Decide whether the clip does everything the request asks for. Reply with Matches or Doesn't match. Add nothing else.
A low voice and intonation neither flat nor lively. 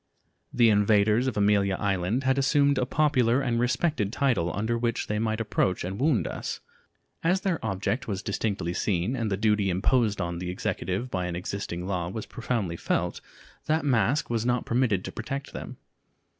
Matches